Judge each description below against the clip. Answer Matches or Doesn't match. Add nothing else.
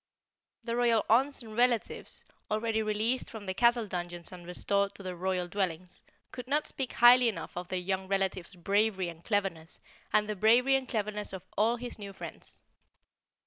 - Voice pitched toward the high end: Matches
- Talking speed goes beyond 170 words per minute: Matches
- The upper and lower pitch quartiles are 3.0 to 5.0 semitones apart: Matches